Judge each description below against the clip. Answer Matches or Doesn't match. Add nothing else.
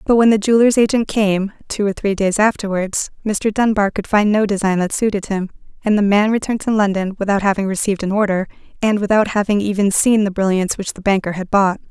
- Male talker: Doesn't match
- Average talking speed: Doesn't match